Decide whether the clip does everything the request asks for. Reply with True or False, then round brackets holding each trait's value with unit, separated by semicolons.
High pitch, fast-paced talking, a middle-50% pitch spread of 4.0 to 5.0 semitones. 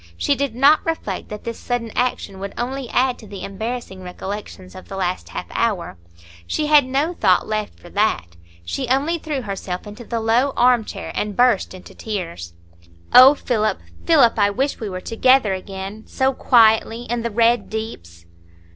False (225 Hz; 170 wpm; 4.6 semitones)